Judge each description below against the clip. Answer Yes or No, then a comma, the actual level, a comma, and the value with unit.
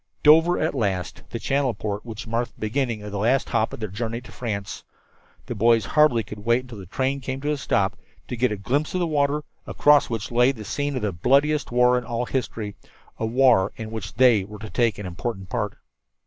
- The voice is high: No, low, 120 Hz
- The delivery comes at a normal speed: No, fast, 225 wpm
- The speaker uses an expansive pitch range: No, average, 4.2 semitones